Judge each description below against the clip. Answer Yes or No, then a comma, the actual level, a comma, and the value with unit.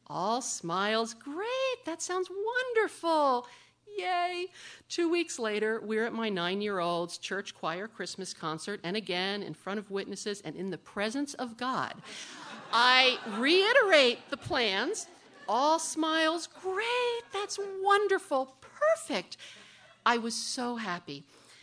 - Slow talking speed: Yes, slow, 130 wpm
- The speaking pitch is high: Yes, very high, 250 Hz